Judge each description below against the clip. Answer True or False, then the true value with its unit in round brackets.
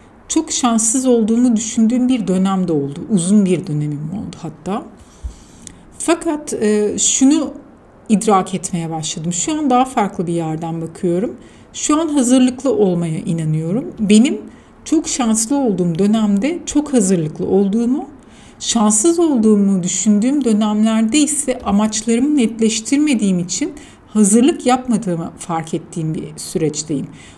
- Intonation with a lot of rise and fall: True (6.0 semitones)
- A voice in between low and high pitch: False (215 Hz)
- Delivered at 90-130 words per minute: True (110 wpm)